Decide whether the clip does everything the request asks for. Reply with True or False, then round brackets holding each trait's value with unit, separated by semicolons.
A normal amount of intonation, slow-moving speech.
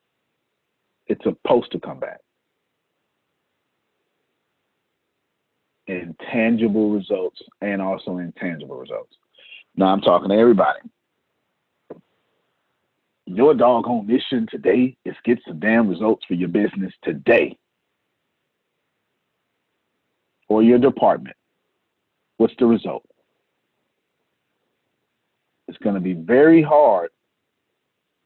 True (4.3 semitones; 90 wpm)